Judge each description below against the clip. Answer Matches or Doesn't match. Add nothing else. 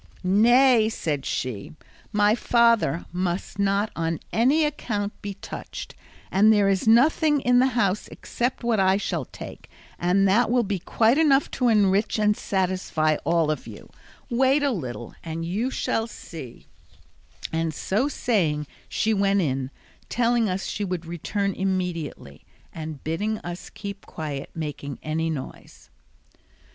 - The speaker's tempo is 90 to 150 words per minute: Matches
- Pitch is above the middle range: Matches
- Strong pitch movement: Matches